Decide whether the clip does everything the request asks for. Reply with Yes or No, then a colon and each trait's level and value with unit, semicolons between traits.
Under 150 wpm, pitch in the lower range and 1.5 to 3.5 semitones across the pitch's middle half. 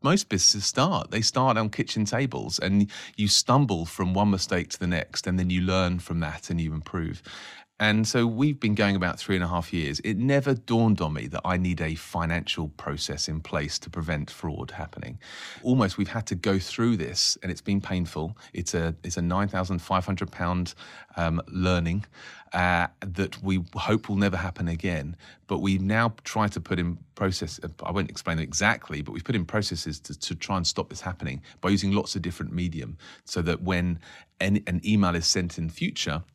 No: average, 200 wpm; very low, 95 Hz; average, 3.2 semitones